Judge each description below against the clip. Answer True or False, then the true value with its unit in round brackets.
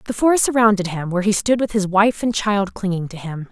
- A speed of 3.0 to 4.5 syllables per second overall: False (5.7 syllables/s)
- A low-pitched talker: False (205 Hz)